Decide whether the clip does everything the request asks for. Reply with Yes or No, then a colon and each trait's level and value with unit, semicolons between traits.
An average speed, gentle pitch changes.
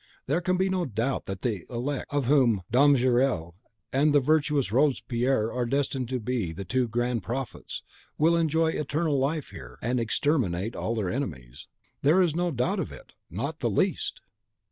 No: average, 175 wpm; average, 4.4 semitones